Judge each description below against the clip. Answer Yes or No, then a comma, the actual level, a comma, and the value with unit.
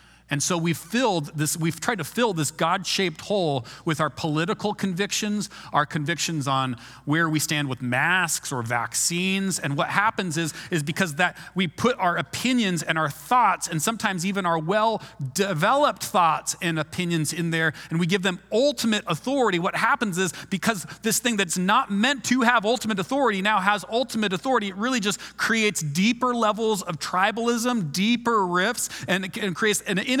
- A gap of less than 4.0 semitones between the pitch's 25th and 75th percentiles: No, average, 5.1 semitones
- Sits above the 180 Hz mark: Yes, high, 190 Hz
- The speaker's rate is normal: Yes, average, 175 wpm